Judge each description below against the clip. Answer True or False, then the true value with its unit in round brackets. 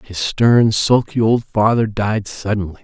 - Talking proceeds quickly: False (150 wpm)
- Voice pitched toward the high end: False (105 Hz)